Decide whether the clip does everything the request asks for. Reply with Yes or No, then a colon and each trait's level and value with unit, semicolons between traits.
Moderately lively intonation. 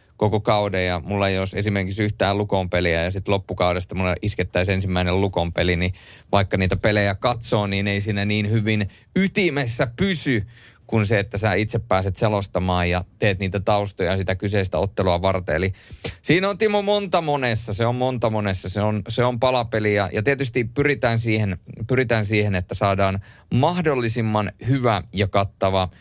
Yes: average, 3.4 semitones